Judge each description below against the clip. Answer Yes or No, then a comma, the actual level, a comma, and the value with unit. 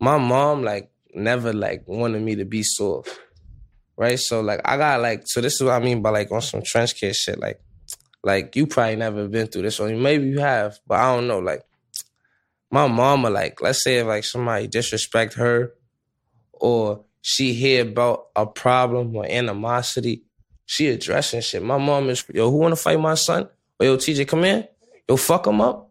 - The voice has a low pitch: Yes, low, 120 Hz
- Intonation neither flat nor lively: Yes, average, 3.0 semitones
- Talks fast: No, average, 195 wpm